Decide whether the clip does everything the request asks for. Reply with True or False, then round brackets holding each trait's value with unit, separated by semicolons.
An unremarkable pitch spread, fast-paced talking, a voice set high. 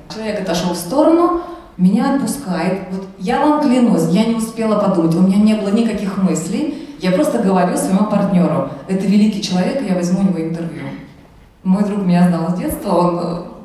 True (4.3 semitones; 175 wpm; 195 Hz)